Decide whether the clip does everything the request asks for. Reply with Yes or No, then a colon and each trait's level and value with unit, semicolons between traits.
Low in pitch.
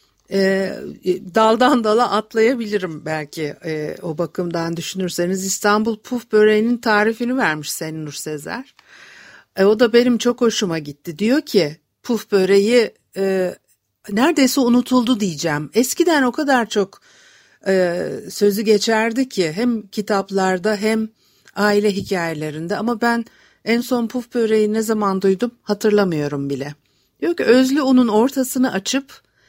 No: high, 210 Hz